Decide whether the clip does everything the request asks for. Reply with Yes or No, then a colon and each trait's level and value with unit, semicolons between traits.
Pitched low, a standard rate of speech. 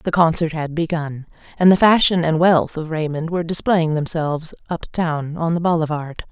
No: medium, 160 Hz; average, 180 wpm